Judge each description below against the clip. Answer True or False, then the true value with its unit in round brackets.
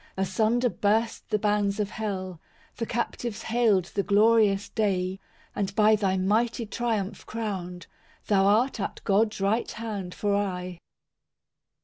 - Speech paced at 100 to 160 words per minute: True (135 wpm)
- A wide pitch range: False (2.4 semitones)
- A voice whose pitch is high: True (205 Hz)